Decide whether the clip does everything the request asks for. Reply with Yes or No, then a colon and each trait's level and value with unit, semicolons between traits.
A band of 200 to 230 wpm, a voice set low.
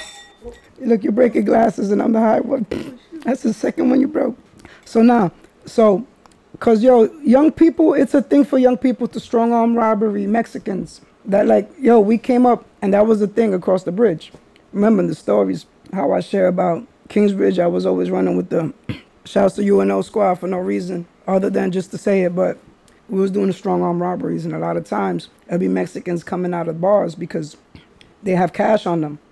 No: fast, 205 wpm; high, 205 Hz